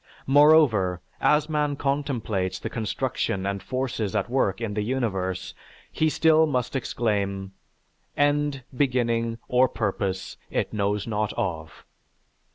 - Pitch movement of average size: No, wide, 5.7 semitones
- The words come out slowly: Yes, slow, 120 wpm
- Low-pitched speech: Yes, low, 115 Hz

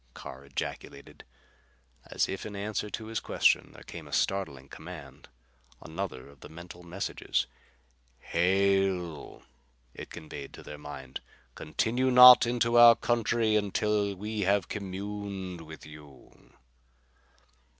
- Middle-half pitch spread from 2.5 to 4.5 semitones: No, average, 5.1 semitones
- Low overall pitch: Yes, very low, 95 Hz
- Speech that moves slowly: Yes, slow, 120 wpm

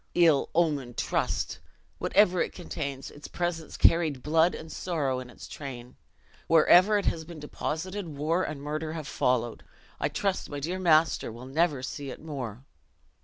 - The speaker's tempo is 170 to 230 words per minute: No, average, 160 wpm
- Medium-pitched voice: Yes, medium, 155 Hz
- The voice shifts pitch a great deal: No, average, 3.8 semitones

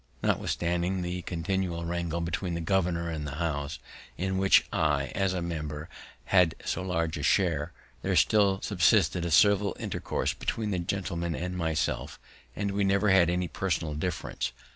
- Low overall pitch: Yes, very low, 85 Hz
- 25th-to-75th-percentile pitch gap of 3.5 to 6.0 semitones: No, average, 2.7 semitones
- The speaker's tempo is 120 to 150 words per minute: No, average, 160 wpm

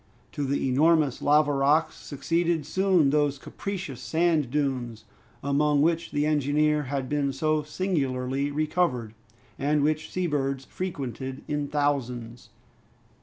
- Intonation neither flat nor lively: No, narrow, 2.3 semitones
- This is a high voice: No, medium, 145 Hz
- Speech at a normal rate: No, slow, 120 wpm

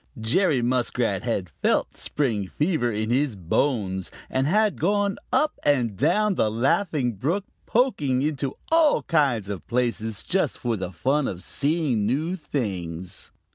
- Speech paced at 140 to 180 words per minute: Yes, average, 145 wpm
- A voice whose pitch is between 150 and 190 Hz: No, low, 130 Hz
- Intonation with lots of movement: Yes, wide, 6.4 semitones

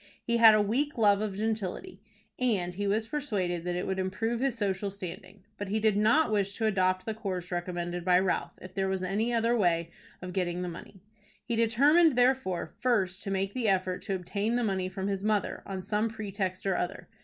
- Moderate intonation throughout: Yes, average, 3.2 semitones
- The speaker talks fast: Yes, fast, 210 wpm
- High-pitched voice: Yes, high, 200 Hz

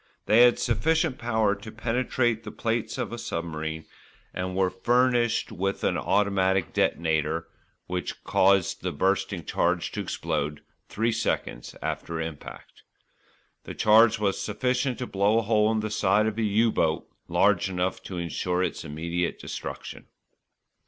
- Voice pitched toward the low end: Yes, low, 100 Hz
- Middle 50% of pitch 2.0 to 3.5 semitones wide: No, average, 4.2 semitones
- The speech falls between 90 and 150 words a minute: Yes, average, 145 wpm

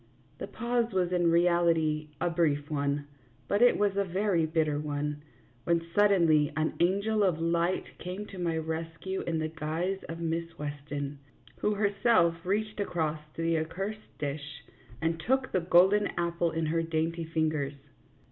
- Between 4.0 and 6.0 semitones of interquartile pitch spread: No, average, 3.2 semitones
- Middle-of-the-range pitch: Yes, medium, 165 Hz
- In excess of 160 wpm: No, average, 155 wpm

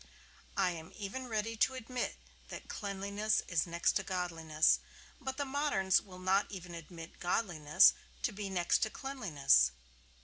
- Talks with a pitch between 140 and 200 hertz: Yes, high, 190 Hz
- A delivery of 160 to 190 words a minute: No, average, 145 wpm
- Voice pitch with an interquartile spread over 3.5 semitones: Yes, average, 4.2 semitones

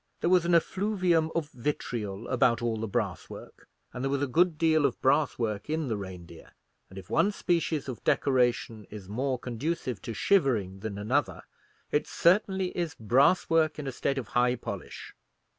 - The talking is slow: No, average, 180 wpm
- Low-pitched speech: Yes, low, 130 Hz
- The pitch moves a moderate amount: No, wide, 6.5 semitones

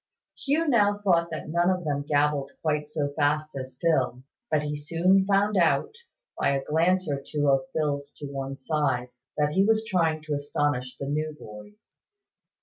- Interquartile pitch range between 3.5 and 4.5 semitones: Yes, average, 3.9 semitones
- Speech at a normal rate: Yes, average, 175 wpm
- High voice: No, medium, 150 Hz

